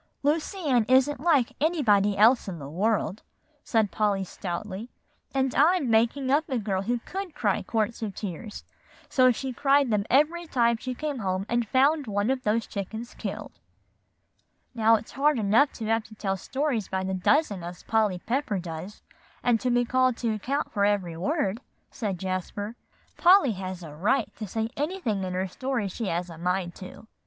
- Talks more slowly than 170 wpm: No, average, 180 wpm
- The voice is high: Yes, high, 225 Hz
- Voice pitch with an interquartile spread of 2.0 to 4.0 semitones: No, wide, 5.4 semitones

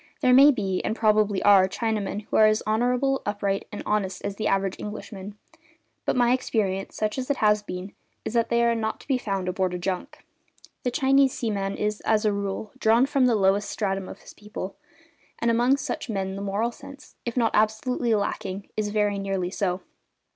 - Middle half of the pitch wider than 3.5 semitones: No, average, 3.1 semitones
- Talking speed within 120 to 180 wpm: No, average, 200 wpm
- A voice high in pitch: Yes, high, 210 Hz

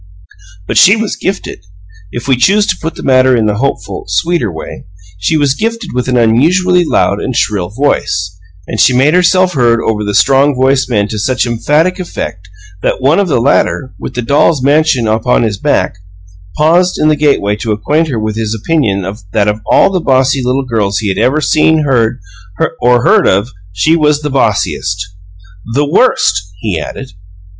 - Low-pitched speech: Yes, low, 130 Hz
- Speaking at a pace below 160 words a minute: No, average, 185 wpm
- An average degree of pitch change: No, wide, 6.2 semitones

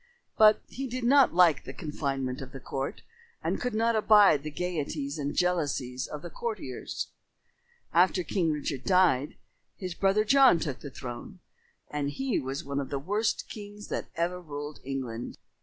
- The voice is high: No, medium, 160 Hz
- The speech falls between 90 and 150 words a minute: No, average, 165 wpm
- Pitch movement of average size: No, wide, 6.7 semitones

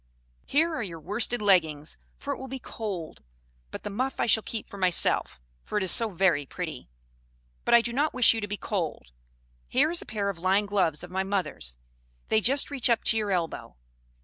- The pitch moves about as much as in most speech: Yes, average, 4.7 semitones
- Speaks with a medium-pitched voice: No, high, 205 Hz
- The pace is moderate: No, fast, 210 wpm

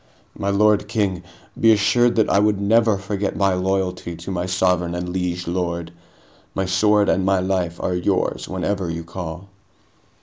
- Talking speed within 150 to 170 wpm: Yes, average, 165 wpm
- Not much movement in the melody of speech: Yes, narrow, 2.3 semitones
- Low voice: Yes, very low, 95 Hz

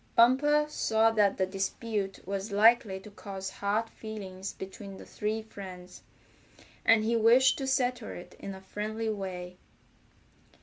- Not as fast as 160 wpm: Yes, average, 140 wpm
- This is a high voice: Yes, high, 210 Hz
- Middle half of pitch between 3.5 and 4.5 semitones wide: No, average, 2.8 semitones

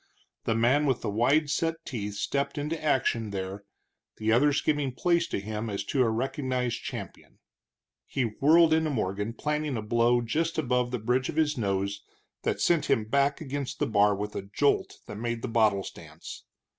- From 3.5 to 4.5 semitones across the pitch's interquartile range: No, average, 5.3 semitones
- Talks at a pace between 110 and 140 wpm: No, average, 180 wpm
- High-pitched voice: No, low, 125 Hz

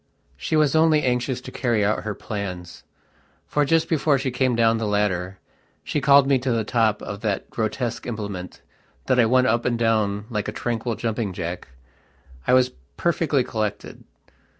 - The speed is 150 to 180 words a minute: Yes, average, 175 wpm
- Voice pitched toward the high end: No, low, 115 Hz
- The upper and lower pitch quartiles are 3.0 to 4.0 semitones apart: Yes, average, 3.7 semitones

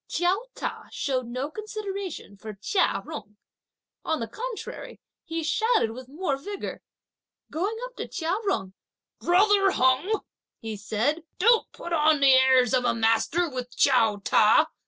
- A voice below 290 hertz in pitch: No, very high, 300 Hz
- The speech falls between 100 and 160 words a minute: Yes, average, 145 wpm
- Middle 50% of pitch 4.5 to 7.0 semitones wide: No, wide, 7.9 semitones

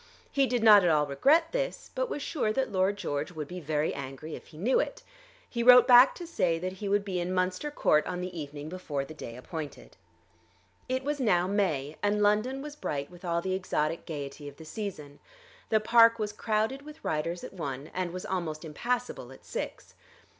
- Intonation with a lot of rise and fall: Yes, wide, 7.0 semitones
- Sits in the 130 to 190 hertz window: Yes, medium, 185 Hz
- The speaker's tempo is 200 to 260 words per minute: Yes, fast, 205 wpm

